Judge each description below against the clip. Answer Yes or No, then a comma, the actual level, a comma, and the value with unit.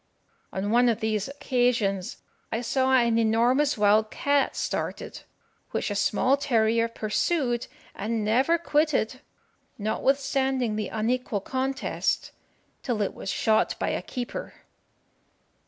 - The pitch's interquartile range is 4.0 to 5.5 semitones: No, average, 3.5 semitones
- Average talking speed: No, slow, 120 wpm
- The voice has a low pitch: No, high, 235 Hz